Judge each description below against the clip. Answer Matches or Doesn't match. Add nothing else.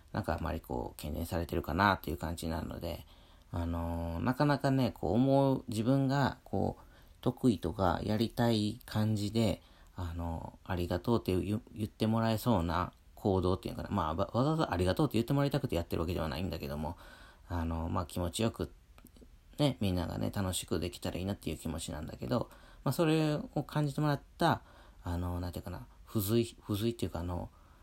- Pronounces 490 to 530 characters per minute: Doesn't match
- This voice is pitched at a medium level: Doesn't match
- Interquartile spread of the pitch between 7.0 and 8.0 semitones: Doesn't match